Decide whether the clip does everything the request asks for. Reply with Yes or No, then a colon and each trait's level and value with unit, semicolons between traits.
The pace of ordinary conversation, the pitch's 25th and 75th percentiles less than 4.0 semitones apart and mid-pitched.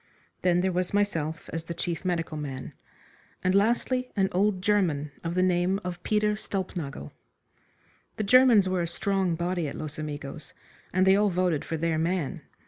Yes: average, 170 wpm; average, 3.3 semitones; medium, 180 Hz